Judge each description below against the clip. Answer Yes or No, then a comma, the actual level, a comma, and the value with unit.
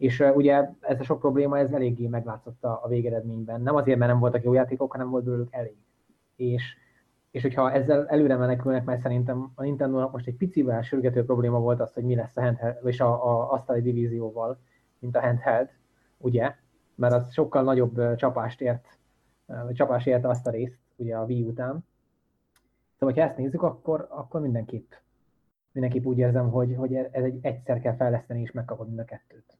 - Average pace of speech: No, fast, 180 wpm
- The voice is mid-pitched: No, low, 125 Hz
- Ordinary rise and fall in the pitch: No, narrow, 1.6 semitones